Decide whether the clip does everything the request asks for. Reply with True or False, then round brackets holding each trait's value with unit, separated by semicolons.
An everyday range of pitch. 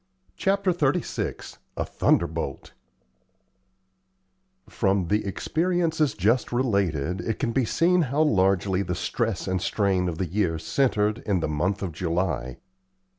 False (6.8 semitones)